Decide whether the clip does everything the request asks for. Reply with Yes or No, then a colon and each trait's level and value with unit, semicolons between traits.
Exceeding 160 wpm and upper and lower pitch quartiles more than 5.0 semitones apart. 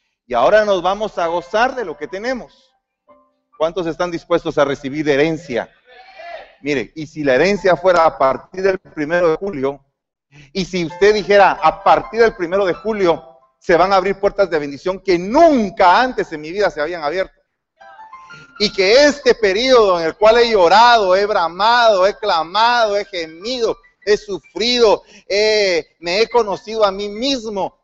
Yes: average, 170 wpm; wide, 5.6 semitones